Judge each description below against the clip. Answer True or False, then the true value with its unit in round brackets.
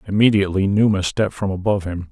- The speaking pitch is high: False (100 Hz)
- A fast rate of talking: False (170 wpm)